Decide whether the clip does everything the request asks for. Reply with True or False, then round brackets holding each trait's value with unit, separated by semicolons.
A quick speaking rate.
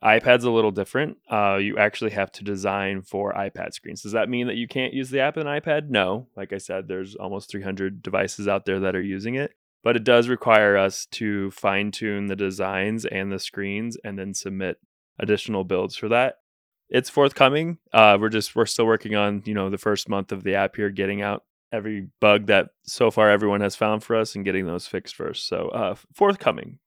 True (215 wpm)